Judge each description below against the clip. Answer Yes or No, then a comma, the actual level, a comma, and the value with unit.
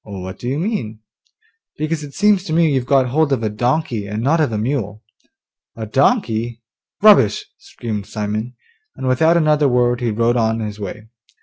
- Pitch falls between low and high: No, low, 120 Hz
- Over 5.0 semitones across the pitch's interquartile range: Yes, wide, 5.6 semitones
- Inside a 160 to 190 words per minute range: Yes, average, 180 wpm